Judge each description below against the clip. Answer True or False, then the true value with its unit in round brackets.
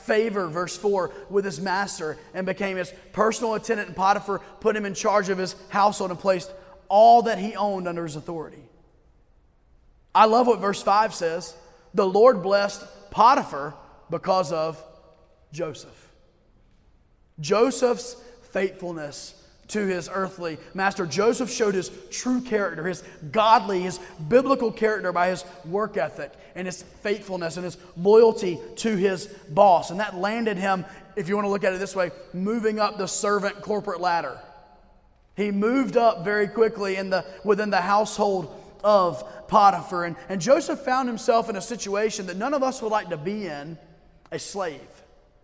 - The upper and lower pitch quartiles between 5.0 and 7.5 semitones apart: False (2.9 semitones)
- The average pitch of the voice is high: True (195 Hz)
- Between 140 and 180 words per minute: True (160 wpm)